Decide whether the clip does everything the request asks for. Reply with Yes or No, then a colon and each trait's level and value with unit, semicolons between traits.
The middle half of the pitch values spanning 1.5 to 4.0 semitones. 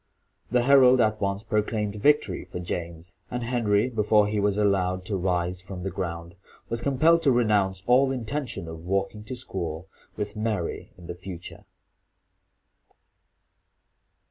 No: average, 4.7 semitones